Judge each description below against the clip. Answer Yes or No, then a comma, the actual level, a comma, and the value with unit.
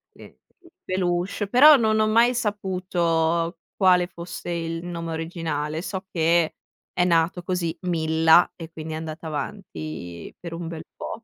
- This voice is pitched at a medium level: Yes, medium, 170 Hz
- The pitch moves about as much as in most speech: No, narrow, 2.3 semitones